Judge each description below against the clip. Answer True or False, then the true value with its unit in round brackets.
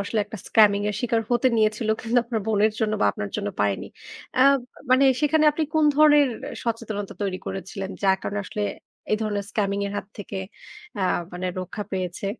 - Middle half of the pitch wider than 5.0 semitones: False (2.9 semitones)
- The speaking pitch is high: True (210 Hz)